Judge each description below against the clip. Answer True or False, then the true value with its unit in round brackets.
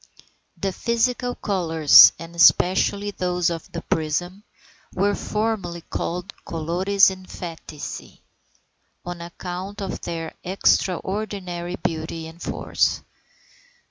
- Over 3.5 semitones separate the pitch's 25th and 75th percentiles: False (2.9 semitones)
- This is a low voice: False (180 Hz)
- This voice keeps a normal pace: False (95 wpm)